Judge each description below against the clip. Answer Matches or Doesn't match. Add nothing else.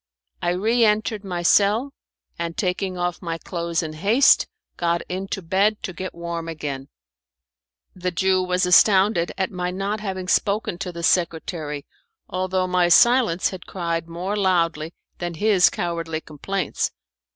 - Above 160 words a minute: Doesn't match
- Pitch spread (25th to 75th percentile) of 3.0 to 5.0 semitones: Doesn't match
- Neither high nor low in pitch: Matches